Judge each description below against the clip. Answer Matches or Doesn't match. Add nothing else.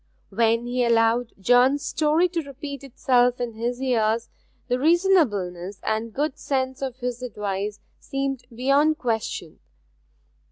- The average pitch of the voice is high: Matches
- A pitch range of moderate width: Matches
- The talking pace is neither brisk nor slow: Doesn't match